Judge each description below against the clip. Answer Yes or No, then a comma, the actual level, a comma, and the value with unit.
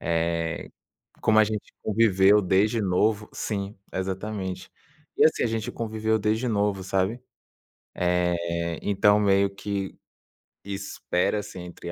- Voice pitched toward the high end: No, low, 100 Hz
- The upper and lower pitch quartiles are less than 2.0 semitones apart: No, average, 2.7 semitones